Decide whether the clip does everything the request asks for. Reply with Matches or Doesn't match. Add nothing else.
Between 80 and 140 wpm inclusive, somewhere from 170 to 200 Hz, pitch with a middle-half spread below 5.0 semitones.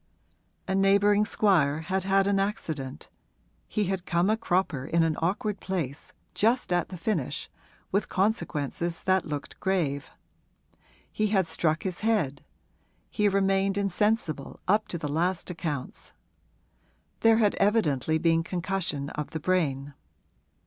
Matches